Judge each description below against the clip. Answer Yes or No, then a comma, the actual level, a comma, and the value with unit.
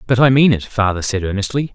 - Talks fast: Yes, fast, 240 wpm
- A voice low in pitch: Yes, low, 115 Hz